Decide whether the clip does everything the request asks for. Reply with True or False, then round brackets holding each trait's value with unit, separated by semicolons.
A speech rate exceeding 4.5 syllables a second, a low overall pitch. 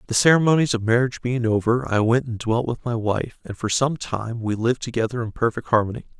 True (6.0 syllables/s; 120 Hz)